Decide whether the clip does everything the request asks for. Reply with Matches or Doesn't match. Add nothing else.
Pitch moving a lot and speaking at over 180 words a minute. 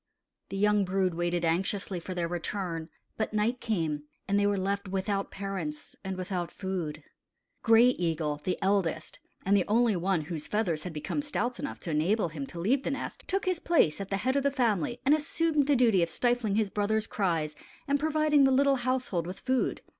Matches